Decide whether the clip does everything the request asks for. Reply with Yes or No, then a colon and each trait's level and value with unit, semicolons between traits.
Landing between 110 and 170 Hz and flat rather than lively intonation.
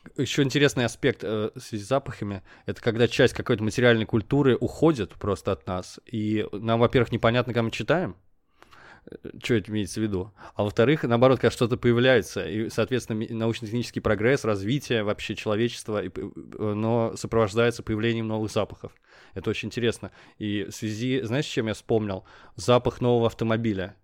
Yes: low, 115 Hz; narrow, 2.2 semitones